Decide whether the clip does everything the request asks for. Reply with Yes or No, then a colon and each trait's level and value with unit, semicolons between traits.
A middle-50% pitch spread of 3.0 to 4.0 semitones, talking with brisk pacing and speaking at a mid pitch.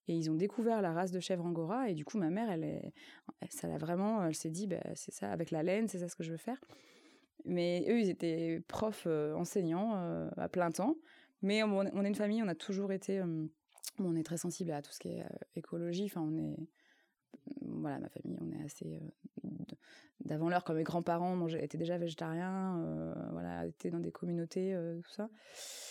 Yes: average, 3.6 semitones; fast, 225 wpm; medium, 175 Hz